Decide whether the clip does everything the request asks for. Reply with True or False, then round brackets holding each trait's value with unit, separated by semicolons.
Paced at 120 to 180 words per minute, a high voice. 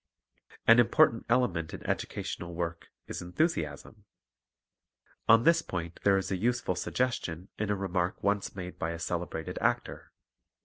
False (145 wpm; 95 Hz)